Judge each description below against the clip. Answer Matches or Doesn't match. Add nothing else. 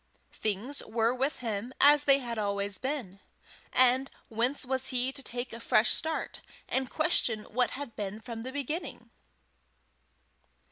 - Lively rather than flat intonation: Doesn't match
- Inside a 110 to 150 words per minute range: Matches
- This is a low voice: Doesn't match